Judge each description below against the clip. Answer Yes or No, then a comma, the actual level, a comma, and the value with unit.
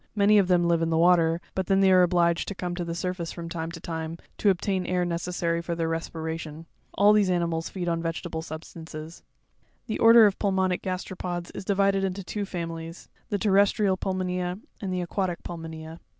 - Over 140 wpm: Yes, average, 200 wpm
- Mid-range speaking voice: Yes, medium, 175 Hz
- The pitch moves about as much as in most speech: No, narrow, 2.3 semitones